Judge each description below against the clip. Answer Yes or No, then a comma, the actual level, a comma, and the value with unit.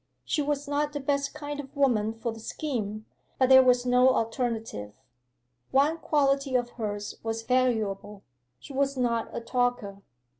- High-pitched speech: Yes, very high, 250 Hz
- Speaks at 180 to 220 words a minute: No, average, 155 wpm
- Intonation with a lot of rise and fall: No, average, 3.8 semitones